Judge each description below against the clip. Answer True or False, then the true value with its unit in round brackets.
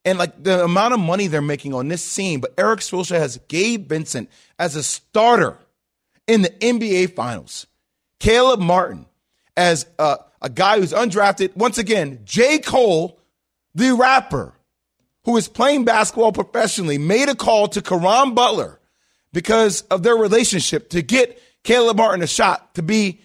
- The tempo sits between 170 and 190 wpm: False (155 wpm)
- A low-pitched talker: False (200 Hz)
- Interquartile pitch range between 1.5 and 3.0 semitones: False (4.9 semitones)